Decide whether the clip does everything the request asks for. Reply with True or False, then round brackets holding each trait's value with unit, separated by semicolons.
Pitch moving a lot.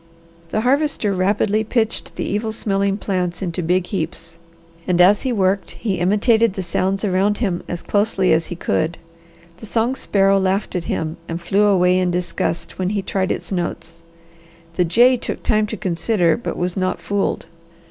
False (2.9 semitones)